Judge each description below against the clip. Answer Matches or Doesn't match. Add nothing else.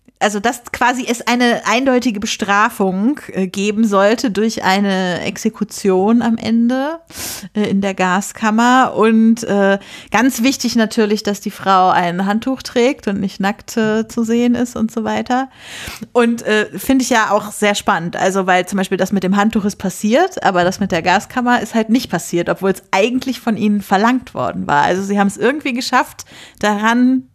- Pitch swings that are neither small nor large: Matches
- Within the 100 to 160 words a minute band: Doesn't match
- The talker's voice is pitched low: Doesn't match